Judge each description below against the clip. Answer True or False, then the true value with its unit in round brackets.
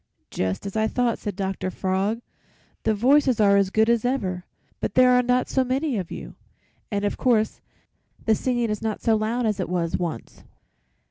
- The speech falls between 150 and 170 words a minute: False (190 wpm)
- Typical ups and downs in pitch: True (4.1 semitones)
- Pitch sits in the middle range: False (220 Hz)